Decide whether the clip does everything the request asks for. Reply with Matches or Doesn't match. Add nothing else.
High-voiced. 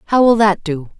Matches